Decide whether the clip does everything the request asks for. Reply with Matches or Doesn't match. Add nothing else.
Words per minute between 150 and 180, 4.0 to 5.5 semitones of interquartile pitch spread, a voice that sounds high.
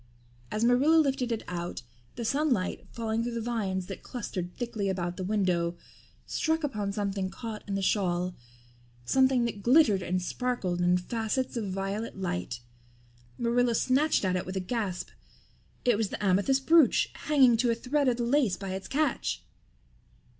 Matches